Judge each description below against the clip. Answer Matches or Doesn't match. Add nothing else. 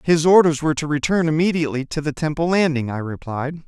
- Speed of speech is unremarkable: Matches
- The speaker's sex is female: Doesn't match